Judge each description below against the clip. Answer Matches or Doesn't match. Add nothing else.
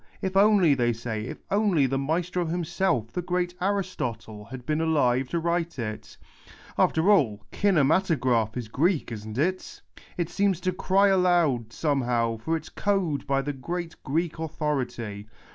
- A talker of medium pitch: Matches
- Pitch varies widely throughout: Matches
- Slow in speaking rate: Doesn't match